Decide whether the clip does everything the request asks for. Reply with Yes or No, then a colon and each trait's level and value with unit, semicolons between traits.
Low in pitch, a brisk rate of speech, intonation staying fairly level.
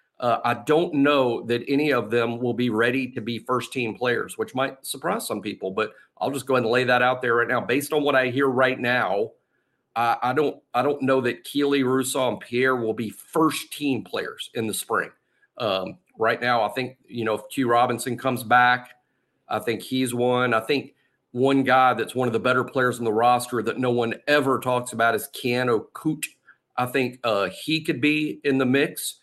Yes: low, 125 Hz; fast, 220 wpm; narrow, 2.2 semitones